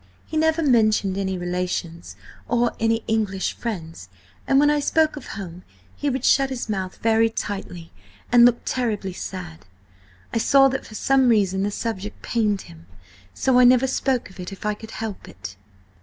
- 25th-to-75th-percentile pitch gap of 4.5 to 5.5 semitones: Yes, average, 4.9 semitones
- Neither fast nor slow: Yes, average, 175 wpm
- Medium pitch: No, high, 220 Hz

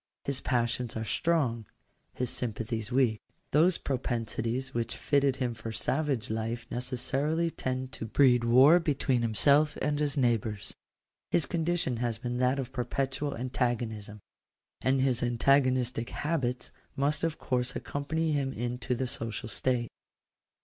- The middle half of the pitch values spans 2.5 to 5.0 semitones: Yes, average, 3.0 semitones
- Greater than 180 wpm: No, slow, 135 wpm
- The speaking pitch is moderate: No, low, 125 Hz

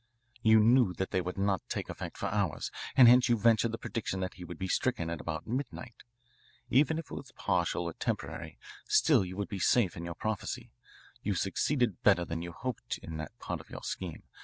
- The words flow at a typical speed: No, fast, 210 wpm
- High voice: No, low, 100 Hz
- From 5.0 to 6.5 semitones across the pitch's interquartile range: Yes, average, 5.3 semitones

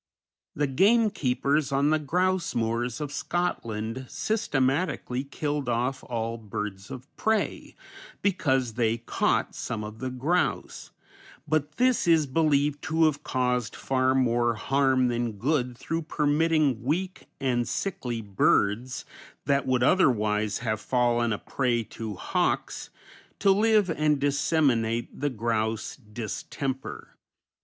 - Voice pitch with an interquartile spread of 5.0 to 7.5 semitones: No, average, 4.5 semitones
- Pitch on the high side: No, low, 130 Hz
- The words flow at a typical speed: No, slow, 120 wpm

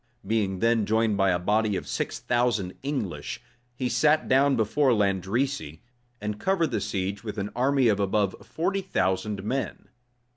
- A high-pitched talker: No, low, 110 Hz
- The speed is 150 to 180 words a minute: Yes, average, 155 wpm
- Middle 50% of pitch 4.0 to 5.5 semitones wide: Yes, average, 4.9 semitones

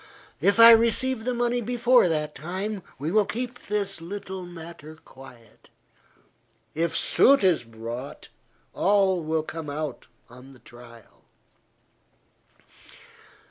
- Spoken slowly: Yes, slow, 115 wpm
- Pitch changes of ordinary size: No, wide, 6.6 semitones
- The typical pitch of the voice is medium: Yes, medium, 175 Hz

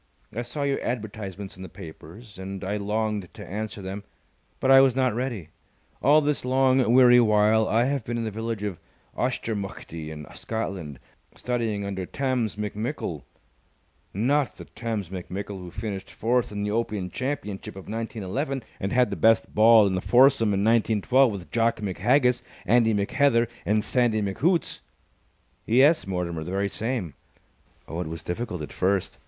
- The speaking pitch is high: No, low, 110 Hz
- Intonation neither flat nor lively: Yes, average, 4.0 semitones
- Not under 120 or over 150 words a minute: No, average, 160 wpm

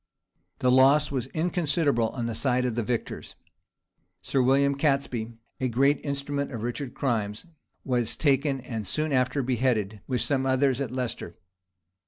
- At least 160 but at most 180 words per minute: No, average, 150 wpm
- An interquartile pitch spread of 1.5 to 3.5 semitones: Yes, average, 2.8 semitones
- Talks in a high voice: No, low, 130 Hz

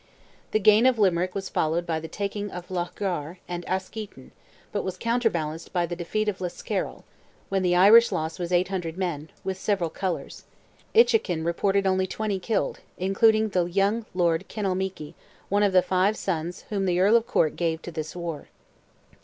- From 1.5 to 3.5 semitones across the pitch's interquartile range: Yes, average, 2.9 semitones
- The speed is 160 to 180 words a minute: Yes, average, 170 wpm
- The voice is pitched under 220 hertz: Yes, medium, 185 Hz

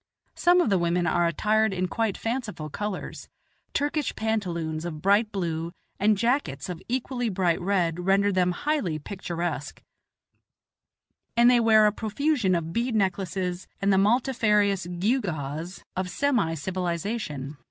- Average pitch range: Yes, average, 4.5 semitones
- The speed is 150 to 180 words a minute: No, slow, 135 wpm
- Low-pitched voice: No, high, 195 Hz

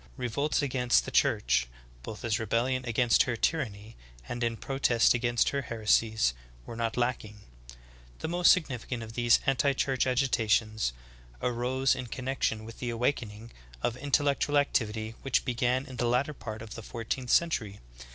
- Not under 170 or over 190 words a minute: No, average, 160 wpm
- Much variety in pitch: No, average, 2.8 semitones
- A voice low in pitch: Yes, low, 120 Hz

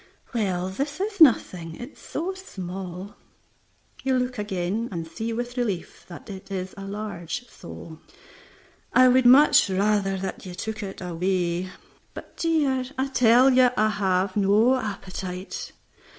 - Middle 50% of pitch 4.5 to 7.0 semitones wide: Yes, average, 5.2 semitones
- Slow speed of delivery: No, average, 150 wpm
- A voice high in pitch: Yes, high, 205 Hz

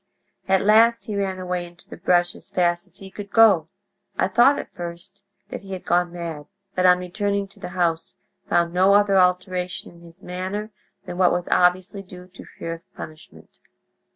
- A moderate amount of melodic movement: No, narrow, 2.0 semitones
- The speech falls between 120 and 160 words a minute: No, average, 190 wpm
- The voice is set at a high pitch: No, medium, 180 Hz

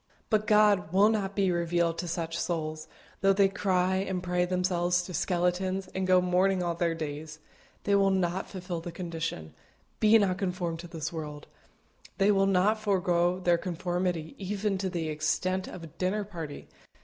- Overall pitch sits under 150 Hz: No, medium, 180 Hz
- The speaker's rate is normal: Yes, average, 175 wpm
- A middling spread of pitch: No, narrow, 2.3 semitones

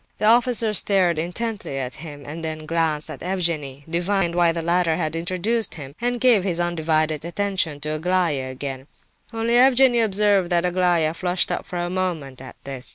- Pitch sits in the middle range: Yes, medium, 175 Hz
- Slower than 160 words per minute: No, average, 175 wpm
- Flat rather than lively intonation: No, average, 3.9 semitones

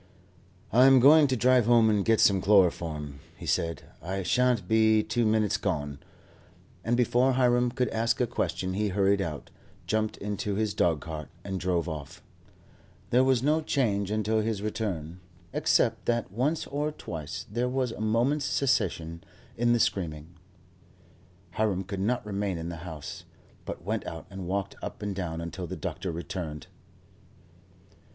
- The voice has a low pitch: Yes, low, 105 Hz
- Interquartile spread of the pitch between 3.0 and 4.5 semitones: No, average, 5.2 semitones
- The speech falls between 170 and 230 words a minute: No, average, 160 wpm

